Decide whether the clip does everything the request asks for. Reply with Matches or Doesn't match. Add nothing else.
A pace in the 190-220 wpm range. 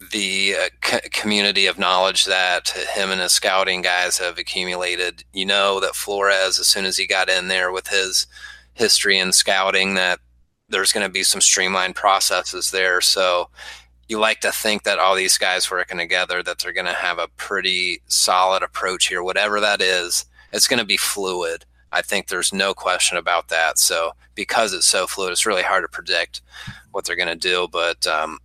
Matches